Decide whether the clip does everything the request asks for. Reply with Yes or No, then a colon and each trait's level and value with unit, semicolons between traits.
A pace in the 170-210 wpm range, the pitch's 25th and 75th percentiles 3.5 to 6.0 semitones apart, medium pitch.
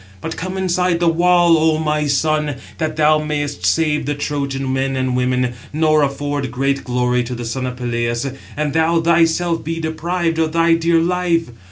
Yes: average, 180 wpm; average, 3.8 semitones; medium, 150 Hz